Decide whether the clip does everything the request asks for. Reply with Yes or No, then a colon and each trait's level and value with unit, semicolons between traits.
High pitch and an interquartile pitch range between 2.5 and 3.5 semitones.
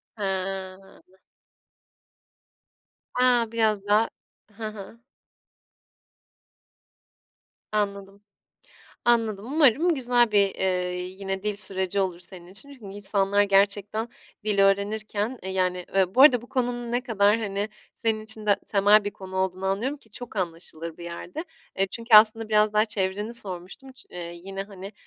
Yes: high, 205 Hz; average, 2.8 semitones